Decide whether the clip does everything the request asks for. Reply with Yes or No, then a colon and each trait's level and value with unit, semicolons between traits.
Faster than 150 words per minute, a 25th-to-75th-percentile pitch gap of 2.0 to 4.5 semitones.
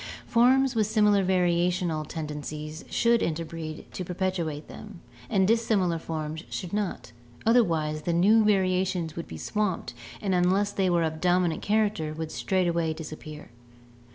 No: slow, 135 wpm; average, 4.2 semitones